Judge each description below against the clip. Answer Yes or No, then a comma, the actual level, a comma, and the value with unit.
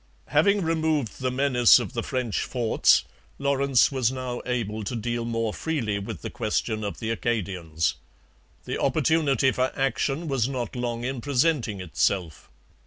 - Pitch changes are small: No, average, 3.6 semitones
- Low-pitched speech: Yes, low, 125 Hz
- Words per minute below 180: Yes, average, 150 wpm